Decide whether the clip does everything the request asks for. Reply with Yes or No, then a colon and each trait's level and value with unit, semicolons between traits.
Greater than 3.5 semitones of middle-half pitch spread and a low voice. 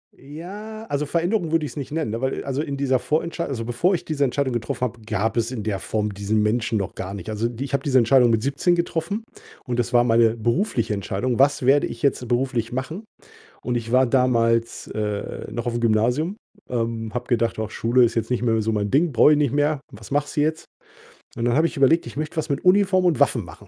Yes: average, 4.5 semitones; low, 125 Hz